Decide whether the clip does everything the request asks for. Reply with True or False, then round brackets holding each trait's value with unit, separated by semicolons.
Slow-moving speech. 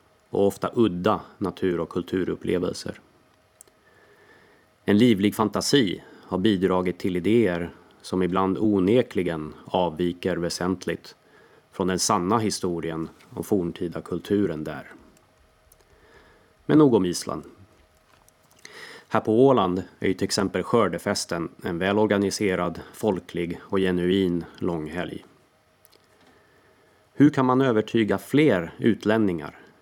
True (100 wpm)